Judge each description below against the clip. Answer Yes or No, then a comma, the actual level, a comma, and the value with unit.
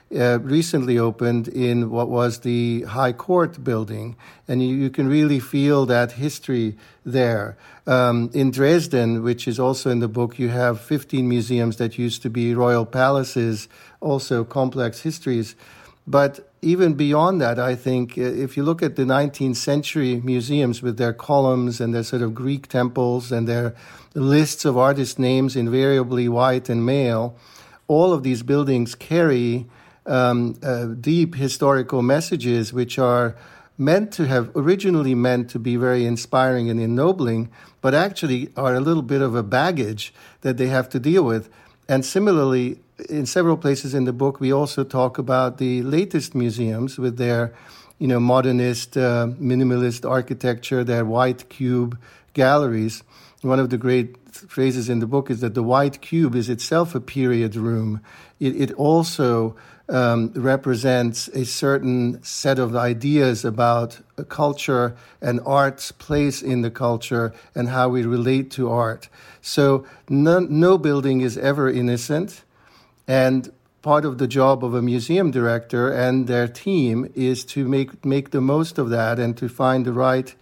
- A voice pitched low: Yes, low, 130 Hz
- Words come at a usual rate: Yes, average, 160 wpm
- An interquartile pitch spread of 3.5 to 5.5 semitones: No, narrow, 2.4 semitones